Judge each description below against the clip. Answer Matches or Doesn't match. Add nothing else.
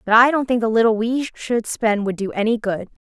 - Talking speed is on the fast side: Matches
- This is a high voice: Matches